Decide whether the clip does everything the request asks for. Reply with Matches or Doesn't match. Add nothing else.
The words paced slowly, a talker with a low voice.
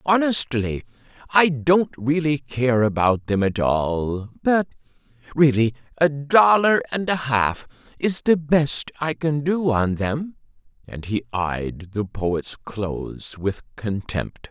Matches